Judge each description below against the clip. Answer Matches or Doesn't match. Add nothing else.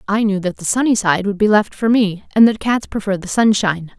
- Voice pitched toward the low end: Doesn't match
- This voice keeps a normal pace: Doesn't match